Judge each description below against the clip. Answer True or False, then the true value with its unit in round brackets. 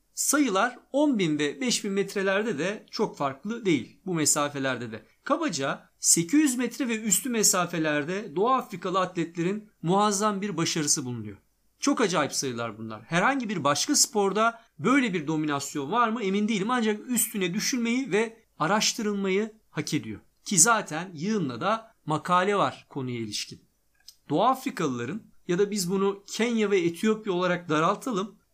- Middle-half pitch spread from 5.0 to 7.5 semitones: True (5.6 semitones)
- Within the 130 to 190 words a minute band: True (140 wpm)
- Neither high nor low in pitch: False (195 Hz)